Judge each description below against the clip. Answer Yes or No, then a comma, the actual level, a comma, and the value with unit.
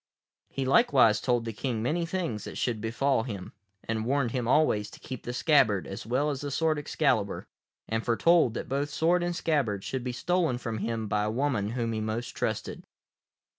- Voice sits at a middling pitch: No, low, 125 Hz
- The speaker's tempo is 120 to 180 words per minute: No, average, 195 wpm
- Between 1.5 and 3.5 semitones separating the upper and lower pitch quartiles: No, average, 4.7 semitones